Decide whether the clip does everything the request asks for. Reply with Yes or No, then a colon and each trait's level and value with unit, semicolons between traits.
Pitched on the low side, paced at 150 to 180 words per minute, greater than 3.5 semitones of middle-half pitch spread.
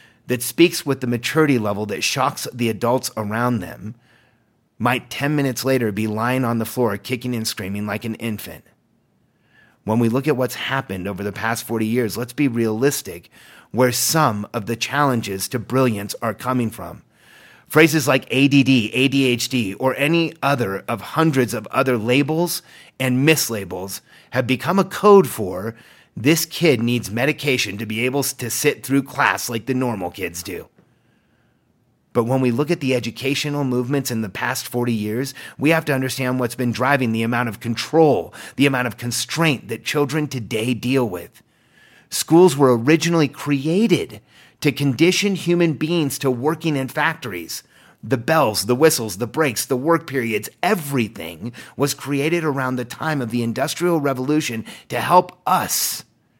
Yes: low, 125 Hz; average, 165 wpm; average, 3.9 semitones